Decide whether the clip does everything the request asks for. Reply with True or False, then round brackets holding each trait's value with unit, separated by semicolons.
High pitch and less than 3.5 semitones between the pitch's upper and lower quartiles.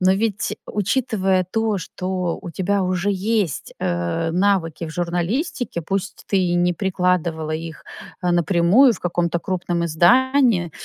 False (180 Hz; 2.9 semitones)